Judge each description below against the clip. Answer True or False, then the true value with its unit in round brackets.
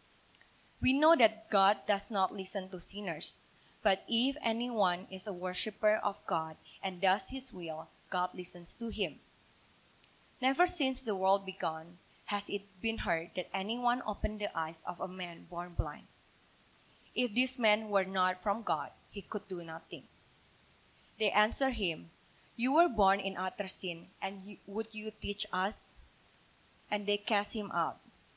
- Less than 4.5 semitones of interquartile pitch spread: True (2.9 semitones)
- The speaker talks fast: False (155 wpm)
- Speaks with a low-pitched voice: False (200 Hz)